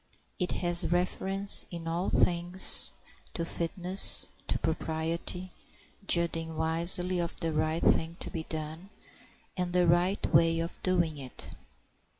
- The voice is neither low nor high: Yes, medium, 170 Hz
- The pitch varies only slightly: Yes, narrow, 1.7 semitones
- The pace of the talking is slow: Yes, slow, 130 wpm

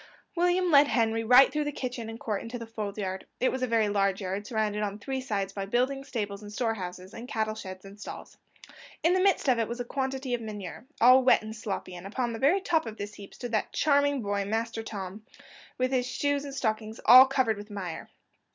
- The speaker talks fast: Yes, fast, 230 wpm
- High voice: Yes, high, 225 Hz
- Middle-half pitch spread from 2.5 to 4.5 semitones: Yes, average, 4.1 semitones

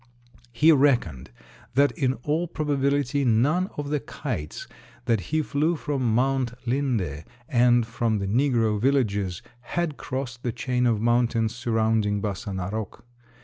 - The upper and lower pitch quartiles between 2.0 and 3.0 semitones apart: No, average, 4.2 semitones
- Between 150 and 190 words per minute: No, slow, 135 wpm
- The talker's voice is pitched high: No, low, 120 Hz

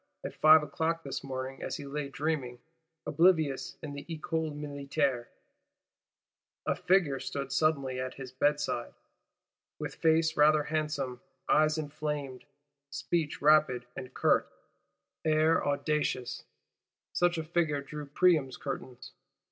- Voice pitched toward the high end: No, medium, 150 Hz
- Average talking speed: No, slow, 120 wpm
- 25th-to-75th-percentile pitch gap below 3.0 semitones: Yes, narrow, 2.6 semitones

